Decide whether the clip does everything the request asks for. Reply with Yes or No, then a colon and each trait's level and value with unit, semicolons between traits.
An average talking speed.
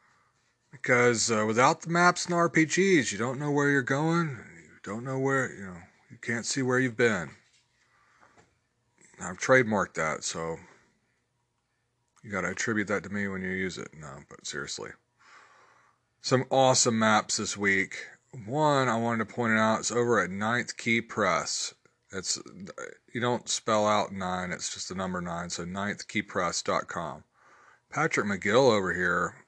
Yes: average, 160 wpm